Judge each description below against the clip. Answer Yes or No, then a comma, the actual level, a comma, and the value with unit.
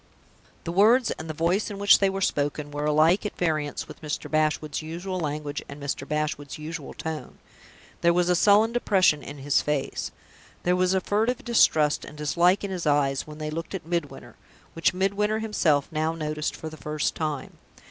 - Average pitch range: Yes, average, 3.9 semitones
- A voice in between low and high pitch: Yes, medium, 160 Hz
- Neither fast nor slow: Yes, average, 190 wpm